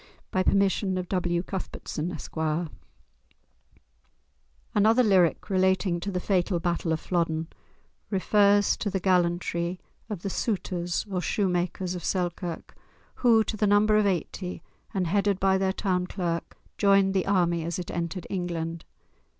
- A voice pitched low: No, medium, 185 Hz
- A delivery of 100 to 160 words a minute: Yes, average, 140 wpm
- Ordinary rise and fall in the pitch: No, narrow, 2.3 semitones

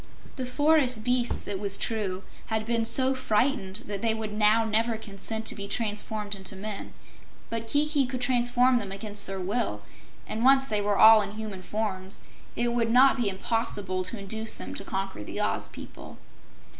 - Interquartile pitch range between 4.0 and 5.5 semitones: No, average, 3.2 semitones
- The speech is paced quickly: No, average, 180 wpm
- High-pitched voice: Yes, high, 220 Hz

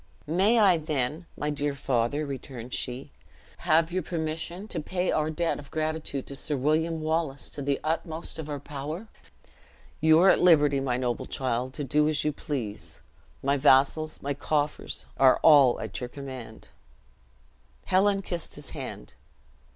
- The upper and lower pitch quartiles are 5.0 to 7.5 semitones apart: No, average, 3.0 semitones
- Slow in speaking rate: No, average, 160 wpm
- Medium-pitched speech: Yes, medium, 150 Hz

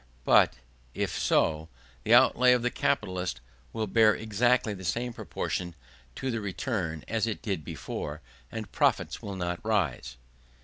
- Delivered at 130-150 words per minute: Yes, average, 145 wpm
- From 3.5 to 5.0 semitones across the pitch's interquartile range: Yes, average, 4.5 semitones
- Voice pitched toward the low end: Yes, low, 100 Hz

